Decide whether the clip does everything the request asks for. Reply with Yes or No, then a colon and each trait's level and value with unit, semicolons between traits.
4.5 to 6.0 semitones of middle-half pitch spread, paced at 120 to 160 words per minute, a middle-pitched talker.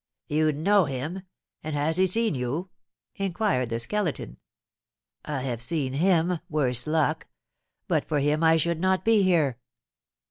Yes: average, 4.8 semitones; average, 145 wpm; medium, 155 Hz